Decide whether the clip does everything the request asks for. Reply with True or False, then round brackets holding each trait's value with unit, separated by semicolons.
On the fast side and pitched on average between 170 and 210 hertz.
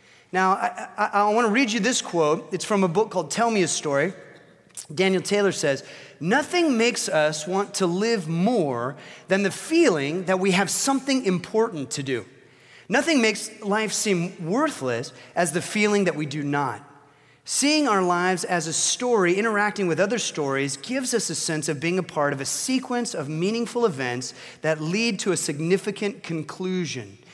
False (180 wpm; 185 Hz)